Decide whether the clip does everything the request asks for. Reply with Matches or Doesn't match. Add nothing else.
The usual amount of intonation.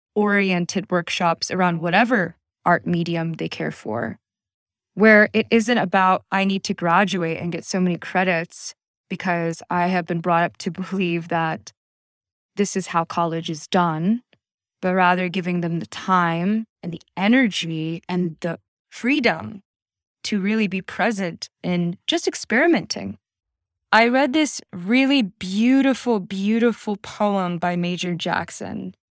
Matches